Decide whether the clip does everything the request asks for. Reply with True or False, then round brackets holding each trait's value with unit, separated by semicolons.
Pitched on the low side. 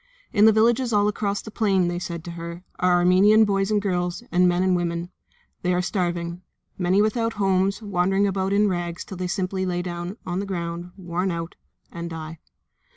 False (185 Hz)